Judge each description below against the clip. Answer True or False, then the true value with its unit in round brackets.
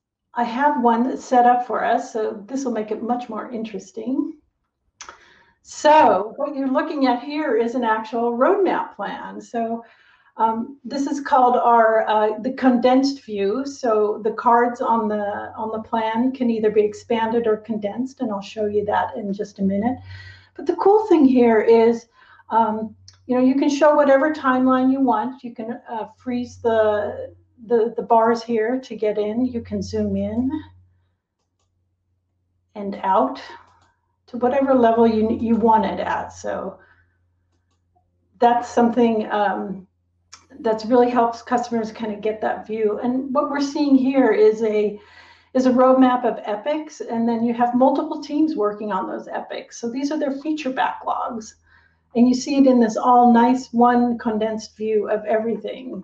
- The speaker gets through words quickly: False (165 wpm)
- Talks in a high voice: True (230 Hz)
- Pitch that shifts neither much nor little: True (3.1 semitones)